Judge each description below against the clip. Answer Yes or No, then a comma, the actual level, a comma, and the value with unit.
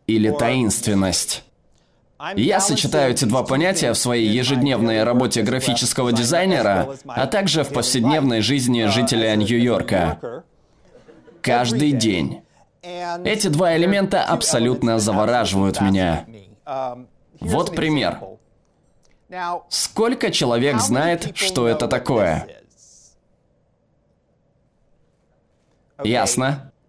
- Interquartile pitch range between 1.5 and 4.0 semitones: No, average, 5.3 semitones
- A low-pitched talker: Yes, low, 125 Hz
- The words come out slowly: Yes, slow, 85 wpm